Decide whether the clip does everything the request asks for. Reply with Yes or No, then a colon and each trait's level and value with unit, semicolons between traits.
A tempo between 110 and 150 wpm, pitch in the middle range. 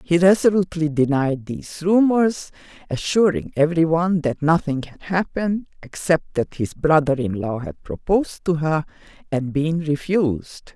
Yes: slow, 135 wpm; medium, 160 Hz